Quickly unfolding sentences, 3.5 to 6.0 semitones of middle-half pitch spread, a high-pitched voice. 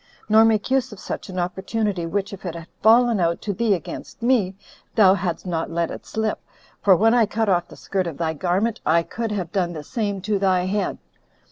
Yes: fast, 220 wpm; average, 3.8 semitones; high, 195 Hz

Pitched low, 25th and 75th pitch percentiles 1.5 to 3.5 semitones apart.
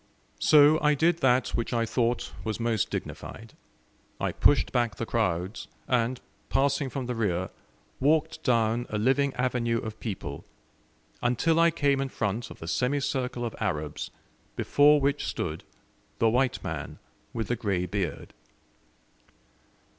No: low, 120 Hz; average, 3.9 semitones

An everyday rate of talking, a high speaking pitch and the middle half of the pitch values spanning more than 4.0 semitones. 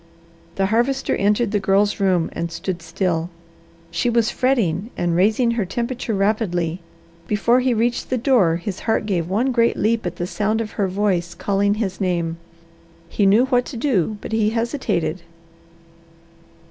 Yes: average, 160 wpm; high, 205 Hz; average, 4.4 semitones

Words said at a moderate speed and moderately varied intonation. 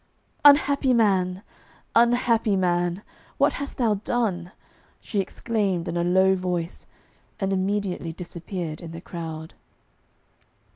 No: slow, 110 wpm; average, 4.1 semitones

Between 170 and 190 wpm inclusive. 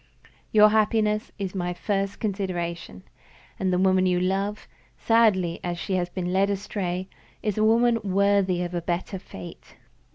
No: average, 155 wpm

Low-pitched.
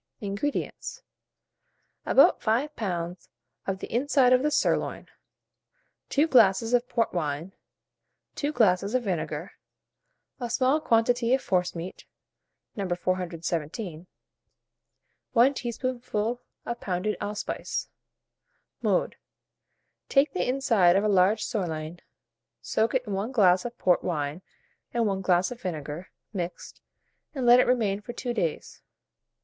No: high, 210 Hz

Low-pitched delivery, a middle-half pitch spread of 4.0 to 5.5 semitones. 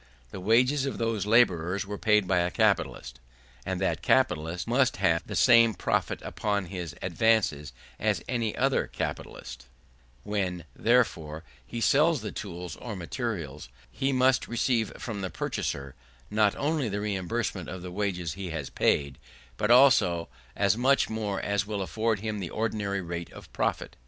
Yes: low, 100 Hz; average, 4.6 semitones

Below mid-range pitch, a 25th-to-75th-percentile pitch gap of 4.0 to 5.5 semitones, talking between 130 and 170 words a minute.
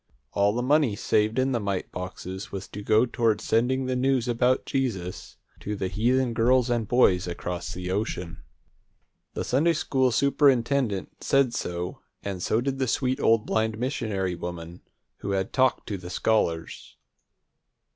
Yes: low, 115 Hz; average, 5.2 semitones; average, 155 wpm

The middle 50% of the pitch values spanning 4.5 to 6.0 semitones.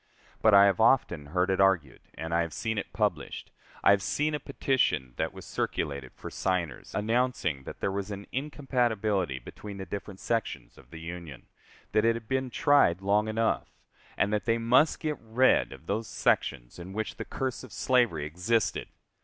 Yes: average, 5.0 semitones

